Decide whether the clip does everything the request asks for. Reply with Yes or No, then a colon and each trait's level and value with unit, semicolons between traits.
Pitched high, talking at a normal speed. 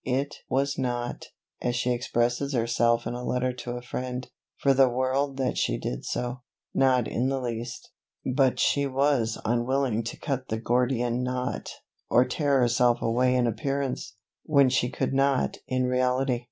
No: low, 125 Hz; average, 165 wpm